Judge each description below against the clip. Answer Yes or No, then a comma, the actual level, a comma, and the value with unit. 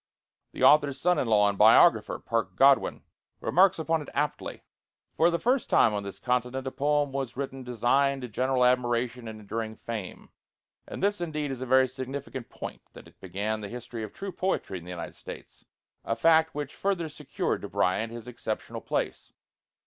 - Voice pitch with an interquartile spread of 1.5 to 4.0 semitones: No, average, 4.5 semitones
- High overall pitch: No, low, 130 Hz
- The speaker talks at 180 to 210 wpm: Yes, average, 185 wpm